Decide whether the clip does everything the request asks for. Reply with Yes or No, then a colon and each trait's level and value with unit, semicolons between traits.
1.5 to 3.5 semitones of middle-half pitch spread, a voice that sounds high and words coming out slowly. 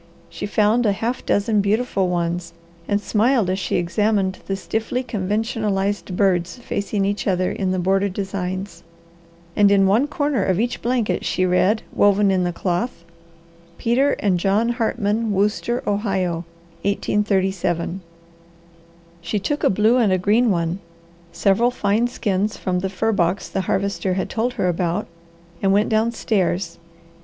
No: average, 2.9 semitones; high, 200 Hz; average, 150 wpm